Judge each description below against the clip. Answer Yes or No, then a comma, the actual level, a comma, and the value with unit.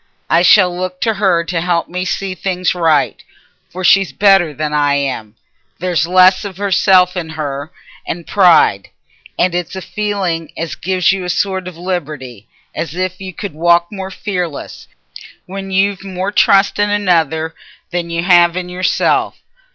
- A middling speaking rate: Yes, average, 165 wpm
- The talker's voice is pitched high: No, medium, 180 Hz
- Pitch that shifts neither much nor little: No, narrow, 2.3 semitones